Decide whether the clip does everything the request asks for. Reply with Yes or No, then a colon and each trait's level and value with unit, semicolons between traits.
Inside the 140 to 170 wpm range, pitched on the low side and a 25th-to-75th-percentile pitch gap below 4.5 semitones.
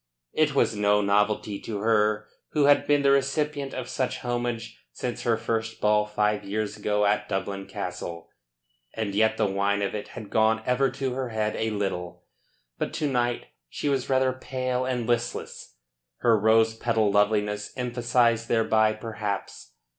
Yes: average, 160 wpm; low, 110 Hz; average, 3.0 semitones